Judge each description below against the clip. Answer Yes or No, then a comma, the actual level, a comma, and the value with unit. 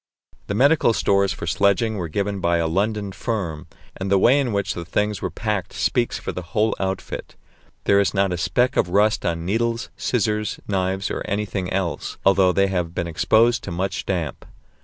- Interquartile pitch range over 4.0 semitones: No, average, 2.9 semitones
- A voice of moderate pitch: No, low, 100 Hz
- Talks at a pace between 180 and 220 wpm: Yes, average, 190 wpm